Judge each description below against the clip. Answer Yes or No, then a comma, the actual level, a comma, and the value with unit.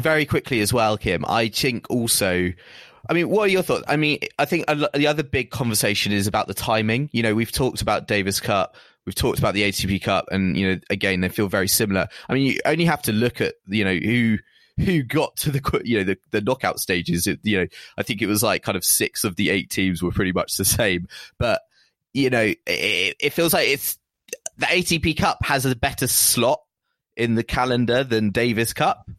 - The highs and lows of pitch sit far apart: Yes, wide, 6.3 semitones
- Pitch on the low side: Yes, low, 115 Hz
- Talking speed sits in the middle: No, fast, 225 wpm